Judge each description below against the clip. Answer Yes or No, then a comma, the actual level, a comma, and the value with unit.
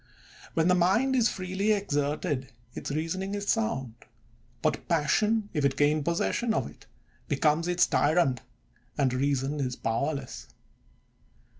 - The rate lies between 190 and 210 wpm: No, slow, 135 wpm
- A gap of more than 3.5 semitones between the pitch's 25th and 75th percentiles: Yes, wide, 5.6 semitones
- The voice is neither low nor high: Yes, medium, 160 Hz